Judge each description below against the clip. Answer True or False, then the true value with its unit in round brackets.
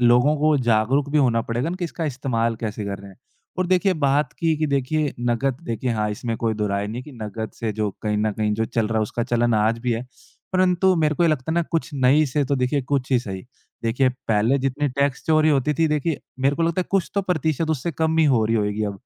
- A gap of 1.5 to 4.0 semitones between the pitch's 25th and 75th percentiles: False (5.3 semitones)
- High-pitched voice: False (130 Hz)